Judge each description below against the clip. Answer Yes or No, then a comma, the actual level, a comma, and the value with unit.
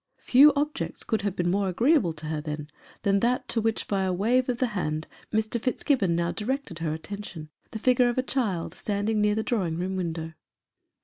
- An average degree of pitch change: No, wide, 6.0 semitones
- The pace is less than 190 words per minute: No, average, 200 wpm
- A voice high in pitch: Yes, high, 205 Hz